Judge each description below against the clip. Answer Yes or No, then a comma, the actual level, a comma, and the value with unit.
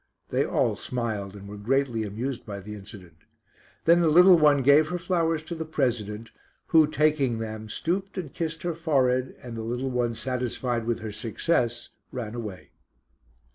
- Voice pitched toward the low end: Yes, low, 125 Hz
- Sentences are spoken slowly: No, average, 170 wpm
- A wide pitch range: Yes, wide, 5.9 semitones